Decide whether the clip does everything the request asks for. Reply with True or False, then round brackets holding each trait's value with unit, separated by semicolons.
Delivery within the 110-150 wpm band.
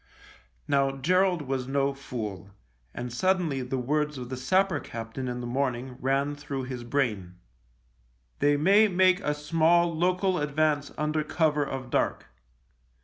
True (145 wpm)